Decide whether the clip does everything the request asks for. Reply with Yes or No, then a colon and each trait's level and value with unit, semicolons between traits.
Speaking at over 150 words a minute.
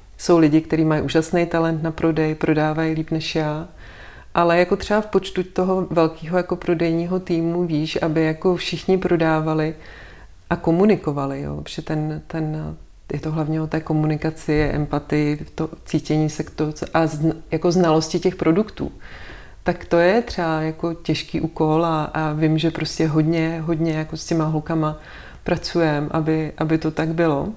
Yes: average, 165 wpm